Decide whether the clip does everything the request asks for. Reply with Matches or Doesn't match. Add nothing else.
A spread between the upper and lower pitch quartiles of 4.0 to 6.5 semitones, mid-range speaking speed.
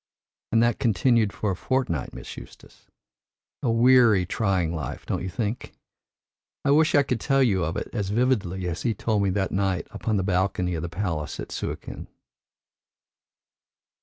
Matches